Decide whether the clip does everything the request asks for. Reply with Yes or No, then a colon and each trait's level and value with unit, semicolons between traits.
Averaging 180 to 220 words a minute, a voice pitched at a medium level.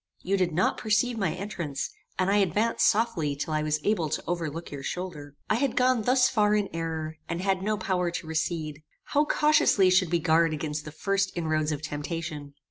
Yes: average, 200 wpm; medium, 175 Hz